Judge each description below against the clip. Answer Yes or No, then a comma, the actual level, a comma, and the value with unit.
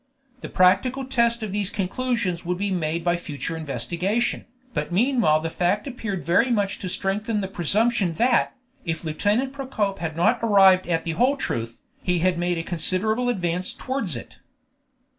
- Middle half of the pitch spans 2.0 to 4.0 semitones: No, average, 5.2 semitones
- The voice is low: No, high, 190 Hz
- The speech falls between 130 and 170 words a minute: Yes, average, 165 wpm